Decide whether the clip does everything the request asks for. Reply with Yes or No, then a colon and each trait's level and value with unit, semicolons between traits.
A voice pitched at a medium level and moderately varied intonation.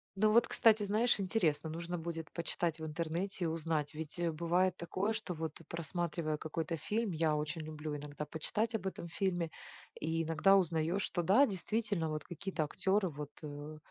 Yes: medium, 170 Hz; average, 3.7 semitones